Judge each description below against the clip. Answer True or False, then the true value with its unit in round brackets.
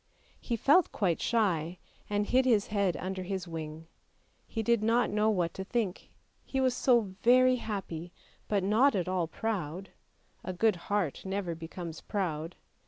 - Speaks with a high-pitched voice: True (195 Hz)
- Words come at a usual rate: True (160 wpm)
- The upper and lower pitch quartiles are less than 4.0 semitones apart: False (4.4 semitones)